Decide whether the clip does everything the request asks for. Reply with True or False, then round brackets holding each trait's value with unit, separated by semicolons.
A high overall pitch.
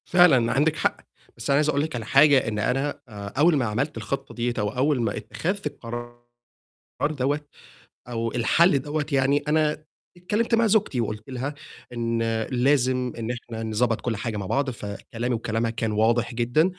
False (125 Hz)